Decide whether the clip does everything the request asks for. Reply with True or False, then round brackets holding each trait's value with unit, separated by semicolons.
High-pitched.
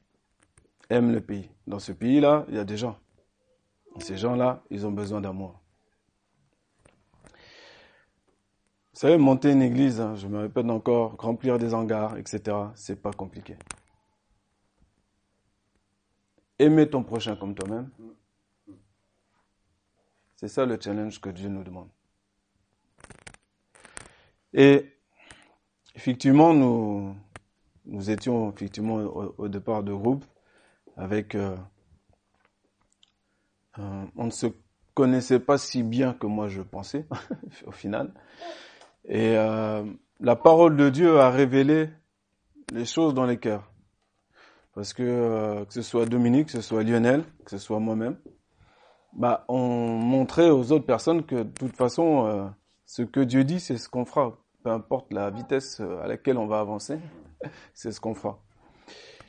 False (110 Hz)